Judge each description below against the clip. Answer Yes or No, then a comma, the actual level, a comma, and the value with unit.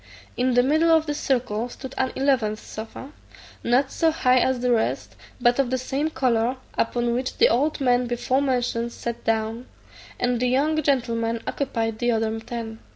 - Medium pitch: No, high, 245 Hz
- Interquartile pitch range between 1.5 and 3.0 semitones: Yes, narrow, 2.4 semitones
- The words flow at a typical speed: Yes, average, 175 wpm